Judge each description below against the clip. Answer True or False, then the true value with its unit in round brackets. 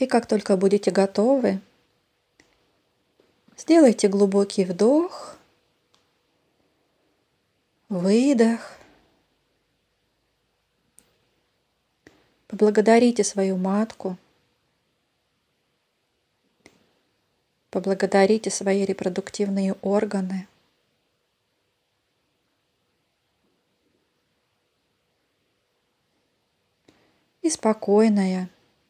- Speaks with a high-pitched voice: True (205 Hz)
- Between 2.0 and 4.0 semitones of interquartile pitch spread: True (2.6 semitones)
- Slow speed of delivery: True (35 wpm)